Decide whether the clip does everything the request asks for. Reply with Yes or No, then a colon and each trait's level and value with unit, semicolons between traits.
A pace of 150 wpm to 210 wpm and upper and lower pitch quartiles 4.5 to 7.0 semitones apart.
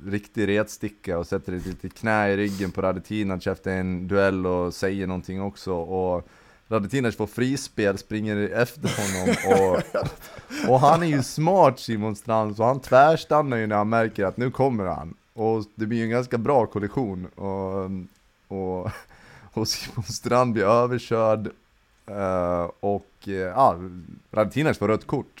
No: average, 155 wpm; average, 3.5 semitones